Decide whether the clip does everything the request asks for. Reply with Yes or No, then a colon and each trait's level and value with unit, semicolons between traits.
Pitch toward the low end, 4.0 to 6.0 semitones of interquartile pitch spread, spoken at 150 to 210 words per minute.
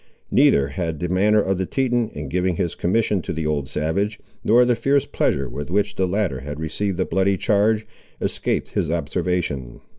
Yes: very low, 90 Hz; average, 5.2 semitones; average, 185 wpm